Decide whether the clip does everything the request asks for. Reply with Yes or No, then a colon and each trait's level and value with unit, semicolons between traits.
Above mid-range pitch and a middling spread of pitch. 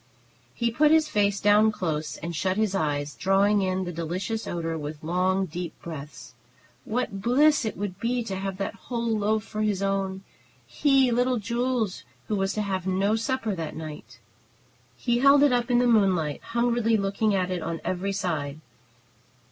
Yes: high, 195 Hz; average, 4.4 semitones